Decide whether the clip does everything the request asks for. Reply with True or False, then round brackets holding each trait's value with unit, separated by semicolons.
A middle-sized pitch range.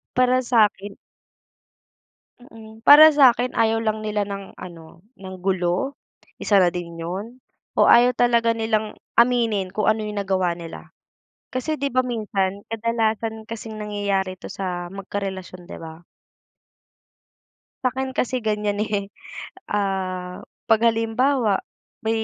True (3.3 semitones)